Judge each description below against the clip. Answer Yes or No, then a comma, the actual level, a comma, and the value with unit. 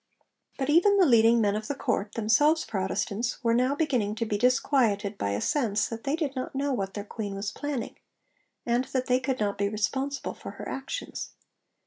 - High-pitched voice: Yes, high, 235 Hz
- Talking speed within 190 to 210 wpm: Yes, average, 195 wpm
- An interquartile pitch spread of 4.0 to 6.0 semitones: Yes, average, 4.8 semitones